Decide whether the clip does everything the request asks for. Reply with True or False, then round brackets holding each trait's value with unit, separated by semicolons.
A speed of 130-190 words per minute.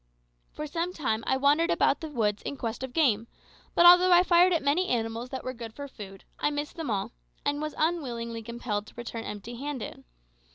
False (205 wpm)